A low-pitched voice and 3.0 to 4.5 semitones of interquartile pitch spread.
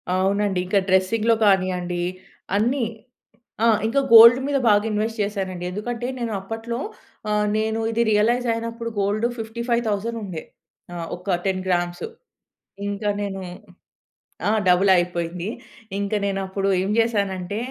No: high, 205 Hz; average, 3.3 semitones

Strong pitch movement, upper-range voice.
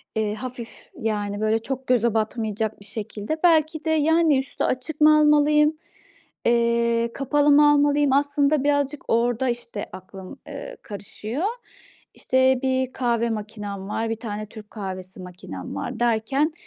No: average, 5.0 semitones; high, 240 Hz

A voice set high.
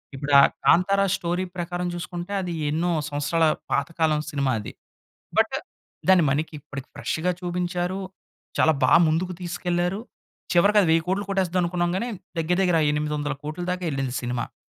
No: medium, 175 Hz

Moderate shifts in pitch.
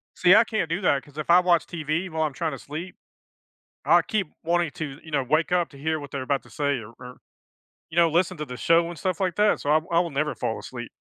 Yes: average, 3.3 semitones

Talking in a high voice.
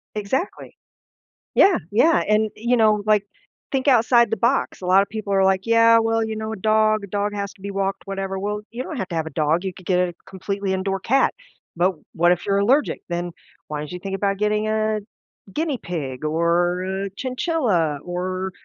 Yes: high, 200 Hz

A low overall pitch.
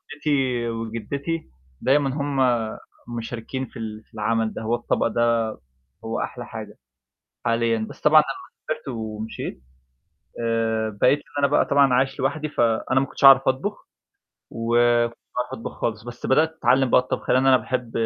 Yes: low, 120 Hz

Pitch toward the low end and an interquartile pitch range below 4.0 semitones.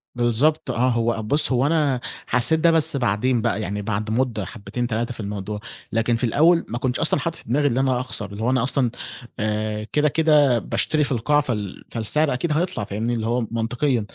No: low, 120 Hz; average, 4.4 semitones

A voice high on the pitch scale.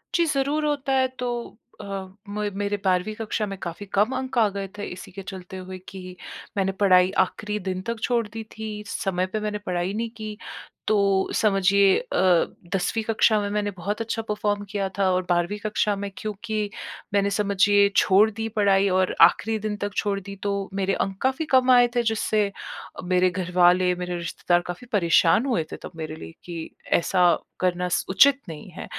Yes: high, 200 Hz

